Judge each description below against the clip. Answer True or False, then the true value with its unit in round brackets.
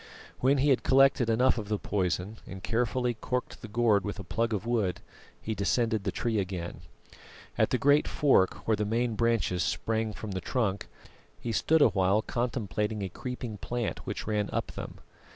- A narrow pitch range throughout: False (3.3 semitones)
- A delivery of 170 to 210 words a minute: True (185 wpm)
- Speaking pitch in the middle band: False (110 Hz)